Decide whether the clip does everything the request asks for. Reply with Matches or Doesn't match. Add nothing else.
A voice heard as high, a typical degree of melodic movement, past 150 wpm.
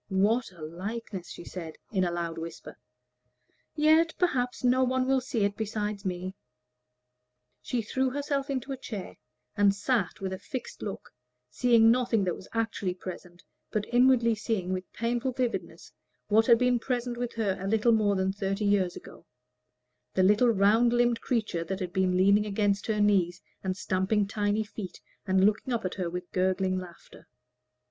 Matches